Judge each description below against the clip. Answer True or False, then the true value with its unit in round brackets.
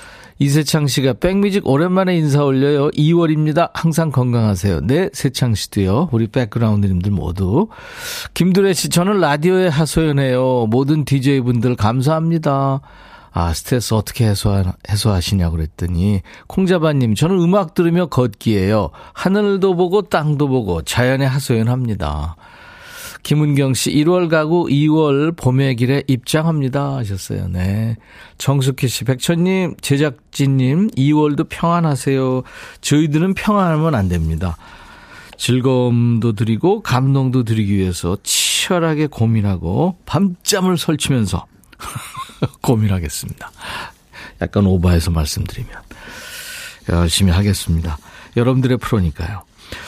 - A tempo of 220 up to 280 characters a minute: False (295 characters per minute)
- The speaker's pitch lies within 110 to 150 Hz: True (135 Hz)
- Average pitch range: False (7.6 semitones)